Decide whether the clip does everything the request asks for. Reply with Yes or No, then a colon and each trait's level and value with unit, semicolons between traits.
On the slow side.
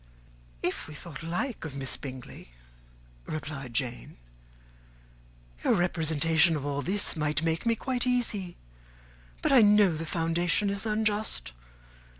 Yes: slow, 130 wpm